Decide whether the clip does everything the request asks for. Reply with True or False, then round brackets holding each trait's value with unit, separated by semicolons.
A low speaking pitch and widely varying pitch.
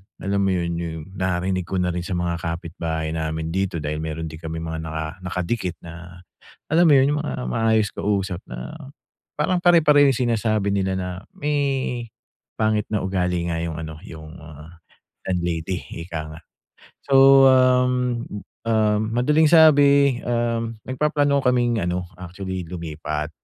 True (95 Hz; 7.0 semitones)